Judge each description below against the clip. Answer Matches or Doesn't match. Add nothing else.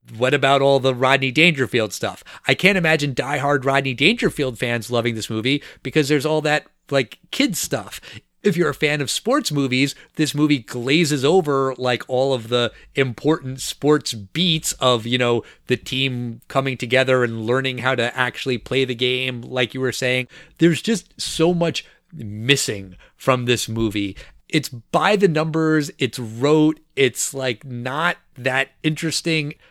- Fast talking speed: Doesn't match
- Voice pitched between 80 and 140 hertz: Matches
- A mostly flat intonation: Doesn't match